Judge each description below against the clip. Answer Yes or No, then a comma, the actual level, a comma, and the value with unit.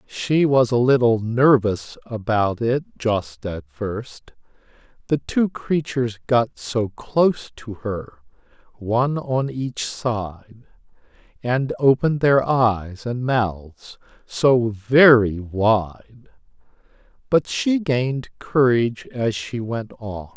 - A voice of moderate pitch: No, low, 120 Hz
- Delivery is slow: Yes, slow, 115 wpm